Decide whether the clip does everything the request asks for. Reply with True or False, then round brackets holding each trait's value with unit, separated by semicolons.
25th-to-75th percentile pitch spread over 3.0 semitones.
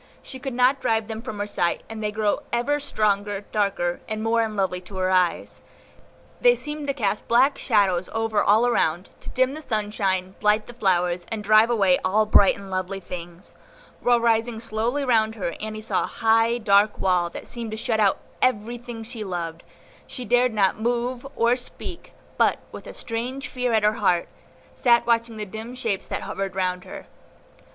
True (3.4 semitones)